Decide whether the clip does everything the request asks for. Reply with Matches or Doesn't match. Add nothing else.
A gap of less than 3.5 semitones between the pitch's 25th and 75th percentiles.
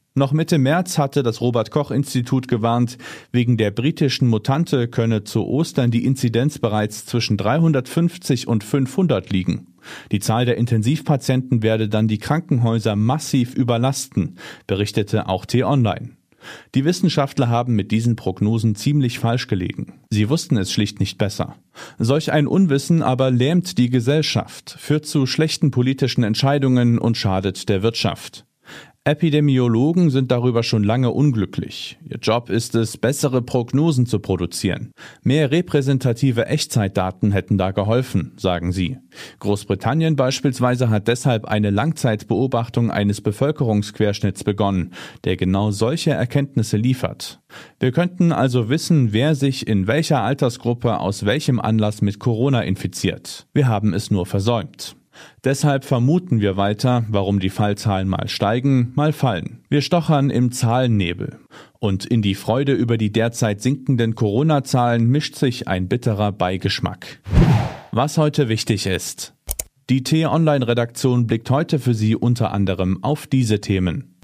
Doesn't match